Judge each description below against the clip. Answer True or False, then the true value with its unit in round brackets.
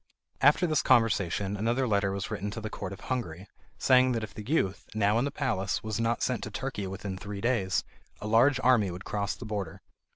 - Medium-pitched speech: False (110 Hz)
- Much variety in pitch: False (4.1 semitones)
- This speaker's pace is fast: True (215 wpm)